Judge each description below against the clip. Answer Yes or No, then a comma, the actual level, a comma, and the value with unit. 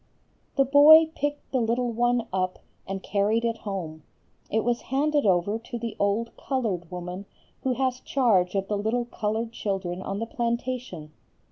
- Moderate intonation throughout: Yes, average, 4.2 semitones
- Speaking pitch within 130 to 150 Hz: No, high, 225 Hz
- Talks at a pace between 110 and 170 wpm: Yes, average, 160 wpm